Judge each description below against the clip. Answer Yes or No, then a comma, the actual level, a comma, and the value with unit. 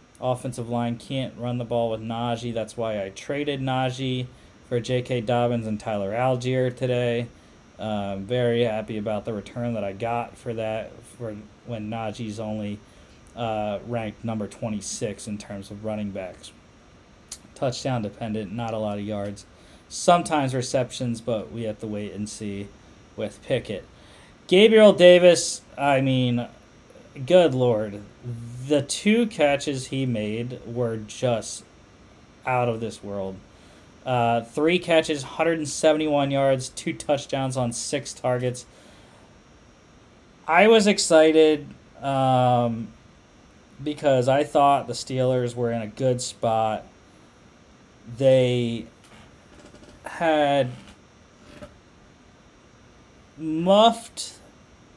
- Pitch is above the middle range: No, low, 120 Hz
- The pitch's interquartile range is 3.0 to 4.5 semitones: Yes, average, 3.7 semitones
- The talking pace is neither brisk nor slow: No, slow, 115 wpm